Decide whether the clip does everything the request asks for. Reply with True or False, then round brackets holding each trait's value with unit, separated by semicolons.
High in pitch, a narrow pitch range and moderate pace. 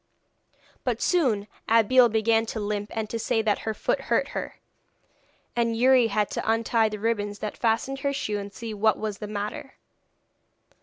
True (220 Hz; 1.7 semitones; 170 wpm)